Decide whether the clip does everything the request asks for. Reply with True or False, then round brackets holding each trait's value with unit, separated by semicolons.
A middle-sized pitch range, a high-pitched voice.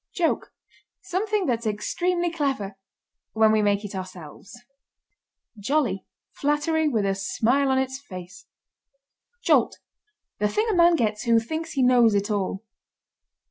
False (7.0 semitones; 235 Hz)